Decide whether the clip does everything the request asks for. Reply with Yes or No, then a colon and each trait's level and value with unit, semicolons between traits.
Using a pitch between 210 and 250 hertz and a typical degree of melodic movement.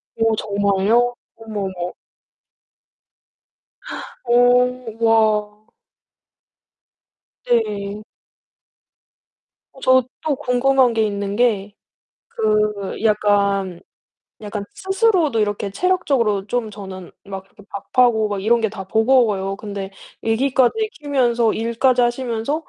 Yes: high, 225 Hz; average, 3.3 semitones